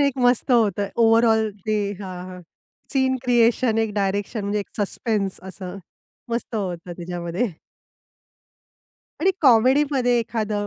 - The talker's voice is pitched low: No, high, 220 Hz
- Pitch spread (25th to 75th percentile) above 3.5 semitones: Yes, average, 3.9 semitones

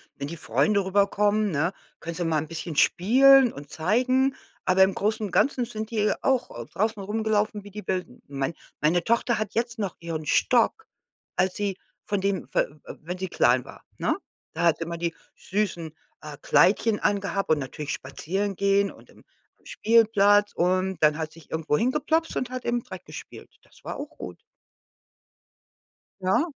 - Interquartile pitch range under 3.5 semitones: No, average, 4.8 semitones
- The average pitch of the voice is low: No, high, 195 Hz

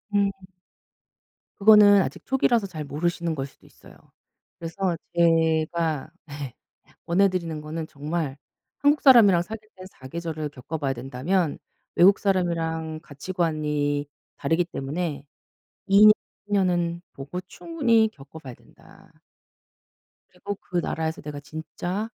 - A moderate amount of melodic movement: Yes, average, 4.1 semitones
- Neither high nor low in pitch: Yes, medium, 165 Hz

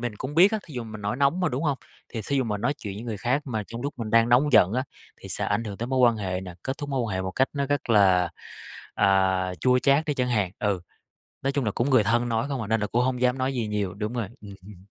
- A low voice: Yes, low, 120 Hz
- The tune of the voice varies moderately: Yes, average, 4.4 semitones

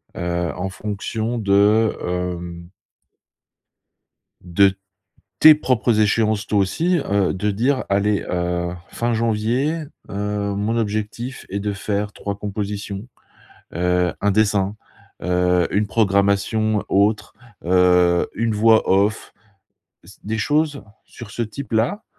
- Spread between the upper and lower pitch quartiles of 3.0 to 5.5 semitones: No, narrow, 2.5 semitones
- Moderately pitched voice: No, low, 105 Hz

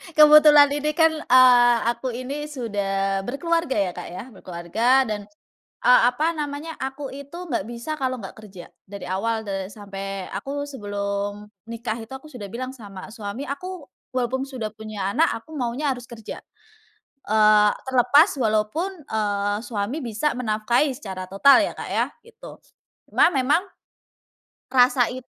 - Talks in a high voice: Yes, high, 240 Hz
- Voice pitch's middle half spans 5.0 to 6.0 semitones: Yes, average, 5.3 semitones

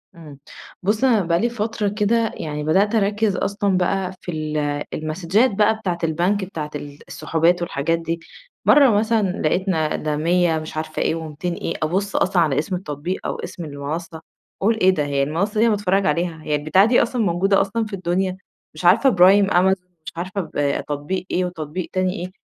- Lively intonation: No, average, 4.1 semitones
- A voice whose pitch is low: No, medium, 180 Hz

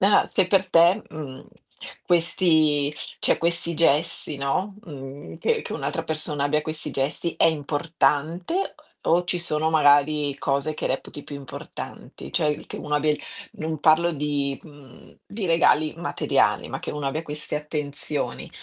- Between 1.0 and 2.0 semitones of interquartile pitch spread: No, narrow, 2.6 semitones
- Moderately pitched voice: Yes, medium, 150 Hz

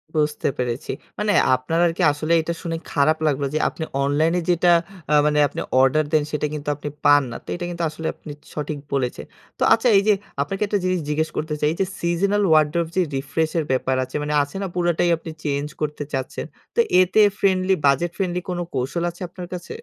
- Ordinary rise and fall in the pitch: Yes, average, 3.2 semitones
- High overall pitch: No, medium, 160 Hz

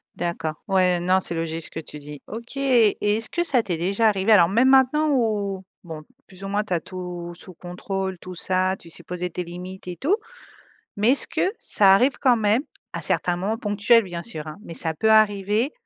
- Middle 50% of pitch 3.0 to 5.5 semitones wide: Yes, average, 4.2 semitones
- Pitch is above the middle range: Yes, high, 195 Hz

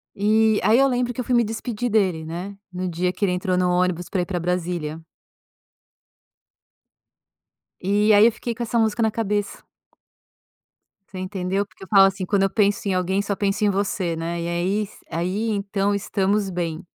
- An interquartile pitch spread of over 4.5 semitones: No, average, 2.7 semitones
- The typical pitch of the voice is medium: No, high, 195 Hz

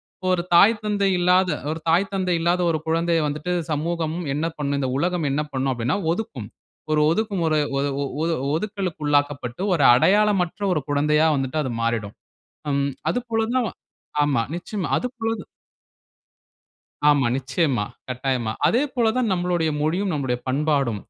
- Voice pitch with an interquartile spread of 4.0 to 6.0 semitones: Yes, average, 4.6 semitones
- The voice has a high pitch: No, medium, 160 Hz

